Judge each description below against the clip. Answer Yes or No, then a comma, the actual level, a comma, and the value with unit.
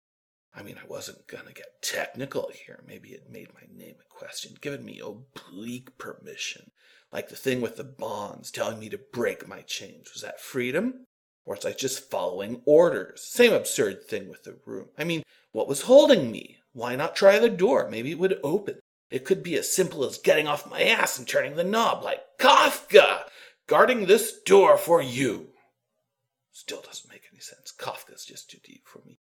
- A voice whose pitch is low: No, very high, 255 Hz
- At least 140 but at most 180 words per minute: No, average, 195 wpm